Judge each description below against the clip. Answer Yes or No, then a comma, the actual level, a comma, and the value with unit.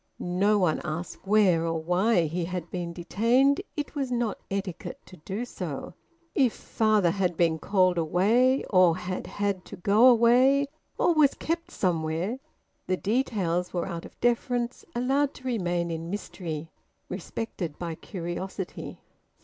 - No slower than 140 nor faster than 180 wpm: Yes, average, 145 wpm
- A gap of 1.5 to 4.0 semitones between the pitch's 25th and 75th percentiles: No, wide, 5.5 semitones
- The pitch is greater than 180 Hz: Yes, high, 190 Hz